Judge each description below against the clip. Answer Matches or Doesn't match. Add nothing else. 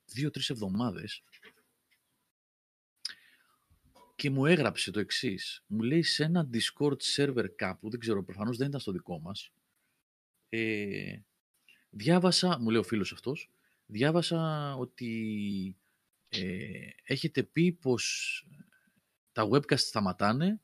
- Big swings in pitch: Matches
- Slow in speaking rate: Matches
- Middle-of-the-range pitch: Doesn't match